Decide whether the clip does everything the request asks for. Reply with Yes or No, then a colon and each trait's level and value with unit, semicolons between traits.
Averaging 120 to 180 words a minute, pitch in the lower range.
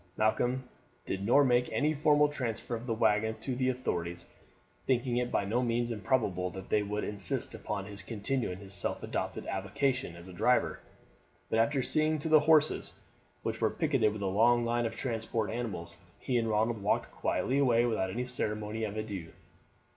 Yes: average, 175 wpm; low, 115 Hz